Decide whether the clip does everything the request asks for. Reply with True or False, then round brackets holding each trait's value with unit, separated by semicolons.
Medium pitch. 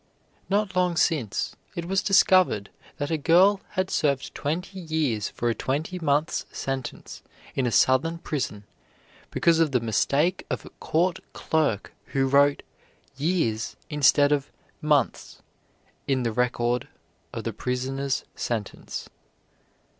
True (145 Hz)